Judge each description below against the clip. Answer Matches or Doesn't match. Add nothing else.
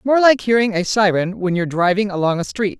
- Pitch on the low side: Doesn't match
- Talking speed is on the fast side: Matches